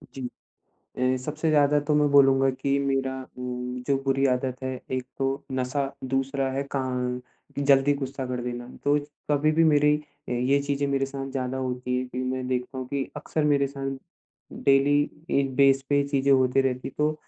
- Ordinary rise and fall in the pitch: No, narrow, 1.5 semitones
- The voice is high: No, low, 135 Hz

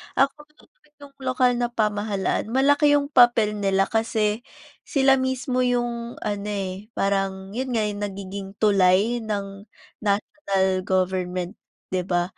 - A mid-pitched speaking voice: No, high, 210 Hz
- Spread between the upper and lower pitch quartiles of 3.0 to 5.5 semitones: Yes, average, 4.4 semitones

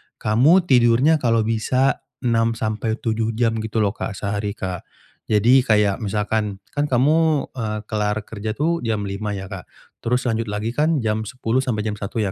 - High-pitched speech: No, low, 115 Hz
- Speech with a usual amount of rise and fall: Yes, average, 3.1 semitones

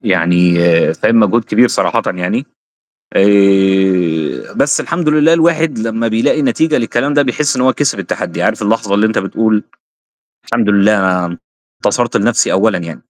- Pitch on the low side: Yes, low, 110 Hz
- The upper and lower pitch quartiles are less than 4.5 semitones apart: No, average, 5.0 semitones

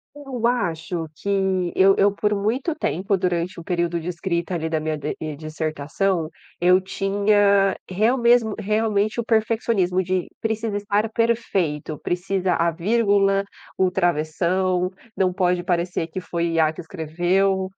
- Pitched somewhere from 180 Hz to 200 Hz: Yes, medium, 185 Hz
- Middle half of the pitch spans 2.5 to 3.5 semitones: Yes, average, 3.1 semitones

